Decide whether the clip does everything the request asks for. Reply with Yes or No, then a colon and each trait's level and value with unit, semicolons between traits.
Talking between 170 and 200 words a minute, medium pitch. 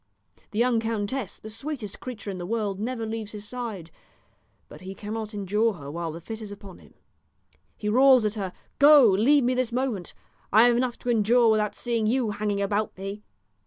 No: average, 195 wpm; high, 215 Hz